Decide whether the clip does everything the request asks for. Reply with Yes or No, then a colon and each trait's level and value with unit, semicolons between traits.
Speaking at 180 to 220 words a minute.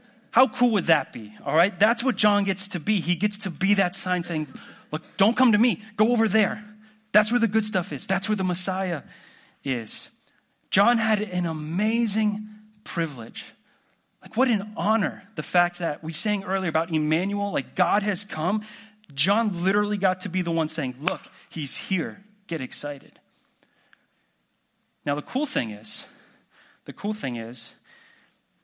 No: average, 170 wpm